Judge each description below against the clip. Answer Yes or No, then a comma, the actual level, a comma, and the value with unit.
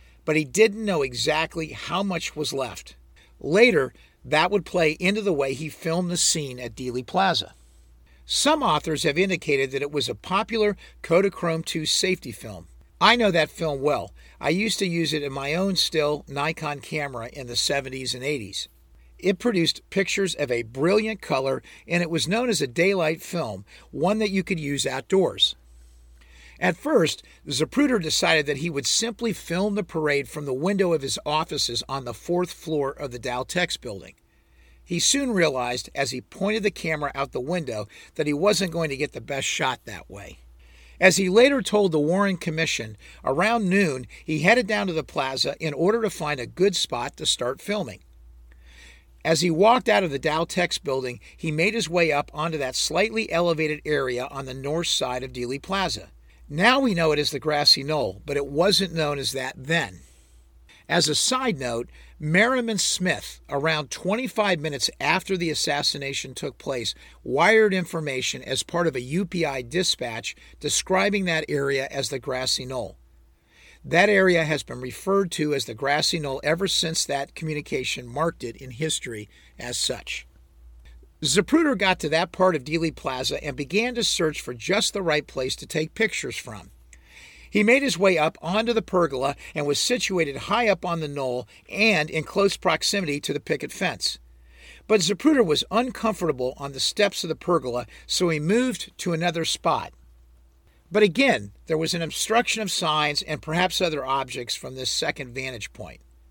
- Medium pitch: Yes, medium, 155 Hz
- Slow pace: No, average, 180 wpm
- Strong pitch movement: Yes, wide, 6.3 semitones